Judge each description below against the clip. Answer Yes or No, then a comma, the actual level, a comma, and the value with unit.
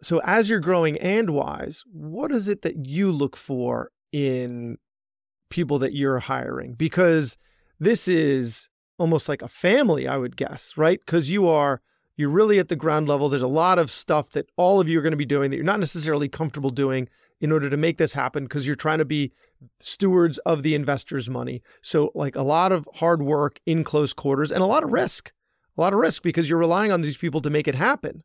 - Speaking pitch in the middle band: Yes, medium, 155 Hz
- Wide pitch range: No, average, 3.3 semitones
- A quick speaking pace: Yes, fast, 220 wpm